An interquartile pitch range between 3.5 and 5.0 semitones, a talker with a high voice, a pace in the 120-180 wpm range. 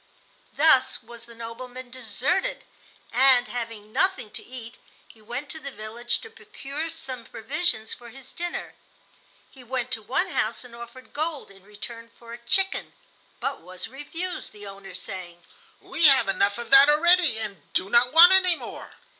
Yes: average, 4.7 semitones; high, 245 Hz; average, 165 wpm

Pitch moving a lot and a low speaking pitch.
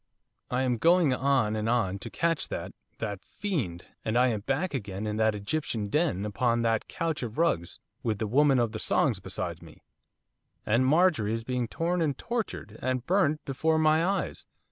Yes: wide, 6.4 semitones; low, 125 Hz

